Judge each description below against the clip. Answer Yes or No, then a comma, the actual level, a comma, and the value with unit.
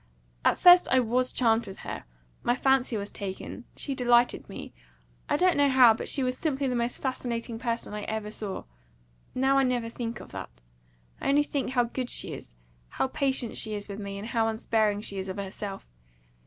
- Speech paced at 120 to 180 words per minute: No, average, 200 wpm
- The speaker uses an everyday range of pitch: Yes, average, 3.6 semitones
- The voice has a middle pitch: No, high, 235 Hz